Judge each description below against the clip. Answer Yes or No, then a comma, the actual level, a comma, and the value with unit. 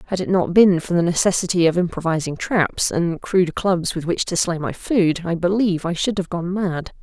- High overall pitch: No, medium, 175 Hz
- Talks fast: Yes, fast, 220 wpm